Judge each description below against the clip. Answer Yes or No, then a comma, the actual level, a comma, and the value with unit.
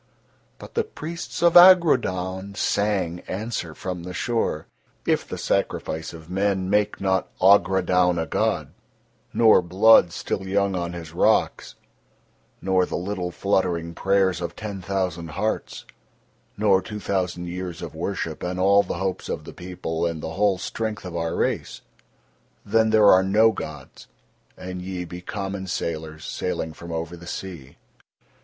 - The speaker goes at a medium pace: Yes, average, 150 wpm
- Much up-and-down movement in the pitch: No, narrow, 2.5 semitones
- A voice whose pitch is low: Yes, very low, 95 Hz